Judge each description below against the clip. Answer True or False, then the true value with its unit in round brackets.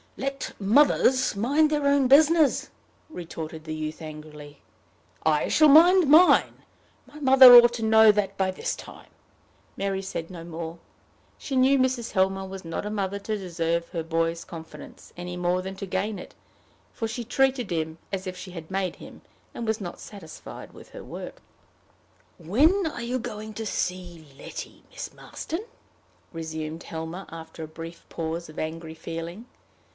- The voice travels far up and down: True (6.7 semitones)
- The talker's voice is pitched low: False (190 Hz)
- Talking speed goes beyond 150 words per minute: True (160 wpm)